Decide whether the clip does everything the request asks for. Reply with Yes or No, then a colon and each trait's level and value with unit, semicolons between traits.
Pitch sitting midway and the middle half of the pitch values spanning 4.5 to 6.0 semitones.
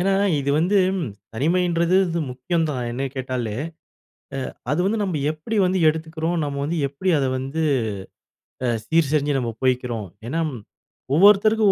Yes: medium, 160 Hz; average, 5.0 semitones